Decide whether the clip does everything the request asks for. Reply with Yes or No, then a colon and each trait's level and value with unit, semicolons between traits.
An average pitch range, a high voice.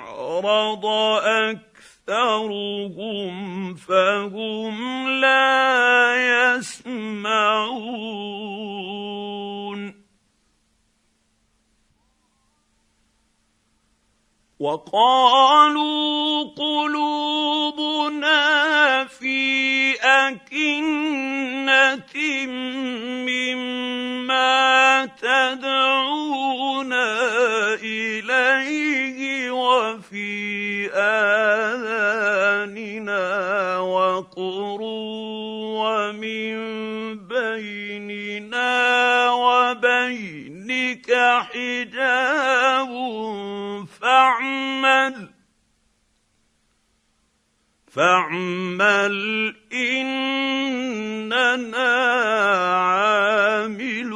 Yes: average, 4.2 semitones; high, 245 Hz